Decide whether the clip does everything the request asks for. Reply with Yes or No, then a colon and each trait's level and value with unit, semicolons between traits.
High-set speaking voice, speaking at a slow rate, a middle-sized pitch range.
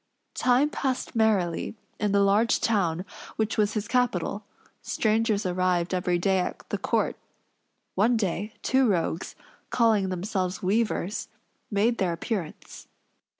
Yes: high, 205 Hz; slow, 125 wpm; average, 3.5 semitones